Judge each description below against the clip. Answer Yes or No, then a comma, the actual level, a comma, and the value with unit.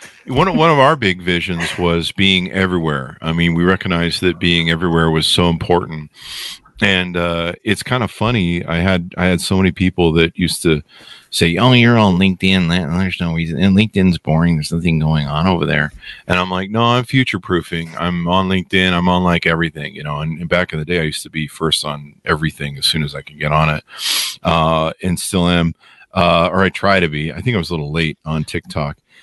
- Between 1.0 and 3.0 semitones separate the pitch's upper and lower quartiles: Yes, narrow, 2.5 semitones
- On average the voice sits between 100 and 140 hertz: No, very low, 85 Hz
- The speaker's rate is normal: No, fast, 220 wpm